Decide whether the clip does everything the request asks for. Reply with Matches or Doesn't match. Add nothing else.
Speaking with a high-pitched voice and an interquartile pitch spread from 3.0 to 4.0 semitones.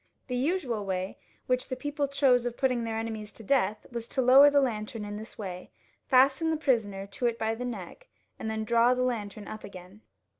Matches